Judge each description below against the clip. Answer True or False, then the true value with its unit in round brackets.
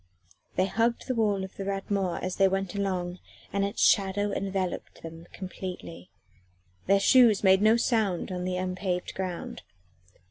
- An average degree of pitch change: False (1.7 semitones)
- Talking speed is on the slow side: False (155 wpm)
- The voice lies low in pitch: False (190 Hz)